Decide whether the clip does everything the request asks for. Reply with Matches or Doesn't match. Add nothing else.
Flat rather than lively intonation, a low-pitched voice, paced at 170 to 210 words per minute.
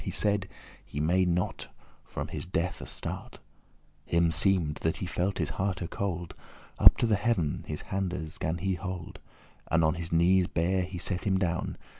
Matches